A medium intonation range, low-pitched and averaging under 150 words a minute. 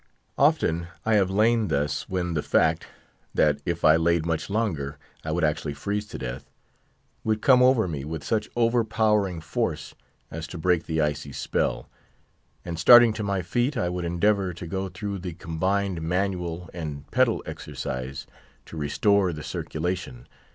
No: average, 4.2 semitones; very low, 90 Hz; average, 160 wpm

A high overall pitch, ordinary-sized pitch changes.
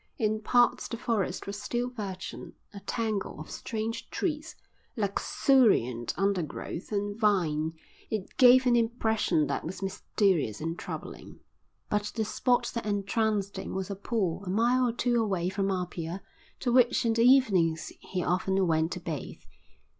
Yes: high, 205 Hz; average, 4.2 semitones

